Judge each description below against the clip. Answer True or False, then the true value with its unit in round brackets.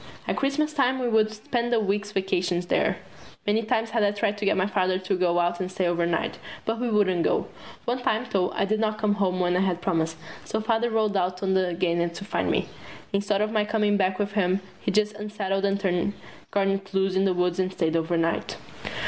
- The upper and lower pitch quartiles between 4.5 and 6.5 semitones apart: False (2.8 semitones)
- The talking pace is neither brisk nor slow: False (220 wpm)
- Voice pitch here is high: True (195 Hz)